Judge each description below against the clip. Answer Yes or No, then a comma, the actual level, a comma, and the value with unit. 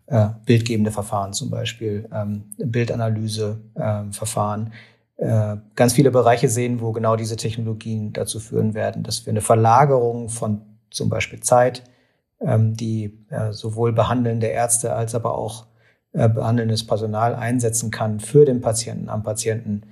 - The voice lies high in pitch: No, low, 115 Hz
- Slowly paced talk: Yes, slow, 120 wpm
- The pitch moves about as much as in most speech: No, narrow, 1.5 semitones